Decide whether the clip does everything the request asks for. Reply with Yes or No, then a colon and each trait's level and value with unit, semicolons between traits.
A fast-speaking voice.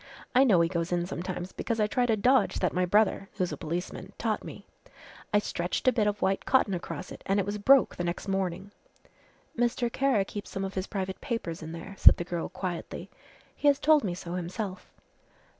Yes: fast, 210 wpm